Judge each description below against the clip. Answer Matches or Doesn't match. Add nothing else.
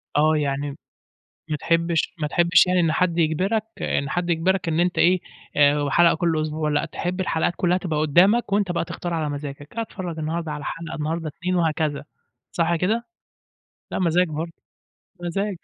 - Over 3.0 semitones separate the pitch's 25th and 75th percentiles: Doesn't match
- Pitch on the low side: Doesn't match